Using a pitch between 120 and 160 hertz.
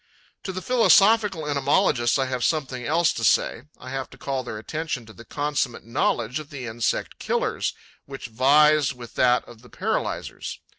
Yes: low, 135 Hz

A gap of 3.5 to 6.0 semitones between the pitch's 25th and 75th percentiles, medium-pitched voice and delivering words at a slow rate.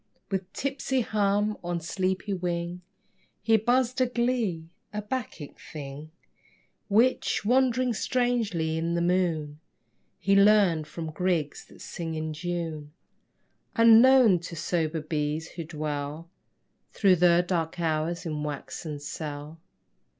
Yes: average, 5.1 semitones; medium, 175 Hz; slow, 120 wpm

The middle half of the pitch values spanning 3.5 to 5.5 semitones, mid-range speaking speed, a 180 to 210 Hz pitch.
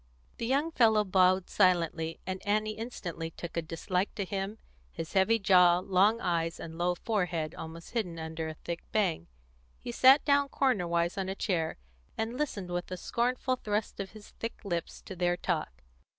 Yes: average, 4.2 semitones; average, 175 wpm; medium, 185 Hz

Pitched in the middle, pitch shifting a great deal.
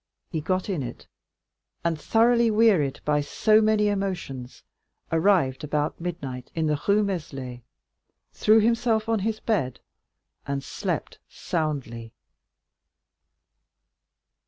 Yes: medium, 170 Hz; wide, 7.1 semitones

